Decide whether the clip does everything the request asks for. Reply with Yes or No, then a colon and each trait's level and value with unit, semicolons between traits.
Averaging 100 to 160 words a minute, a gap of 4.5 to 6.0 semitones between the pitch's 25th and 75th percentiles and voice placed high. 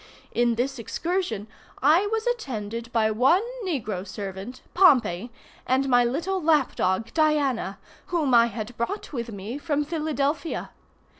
Yes: slow, 135 wpm; wide, 5.6 semitones; very high, 260 Hz